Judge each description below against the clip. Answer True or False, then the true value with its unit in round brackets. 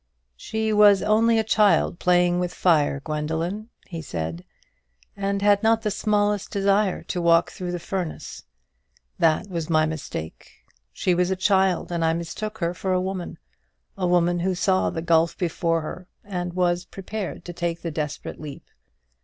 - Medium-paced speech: True (165 wpm)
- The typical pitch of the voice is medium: True (180 Hz)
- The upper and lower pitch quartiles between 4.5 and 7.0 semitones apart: False (3.0 semitones)